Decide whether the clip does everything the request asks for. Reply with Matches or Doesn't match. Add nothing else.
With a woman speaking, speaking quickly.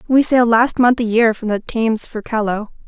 Matches